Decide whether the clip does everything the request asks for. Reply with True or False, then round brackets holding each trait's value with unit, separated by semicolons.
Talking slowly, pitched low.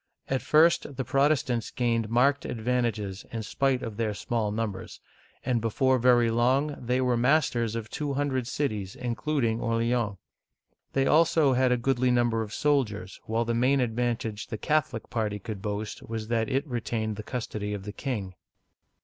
False (165 wpm; 120 Hz)